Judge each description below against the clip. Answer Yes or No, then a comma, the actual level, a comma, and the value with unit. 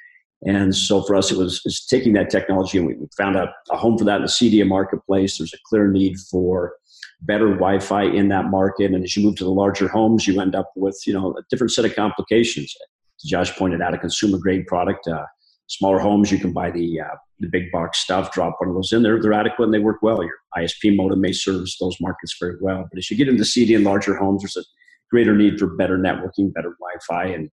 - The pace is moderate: No, fast, 240 wpm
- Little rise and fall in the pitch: Yes, narrow, 2.0 semitones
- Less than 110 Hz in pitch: Yes, very low, 95 Hz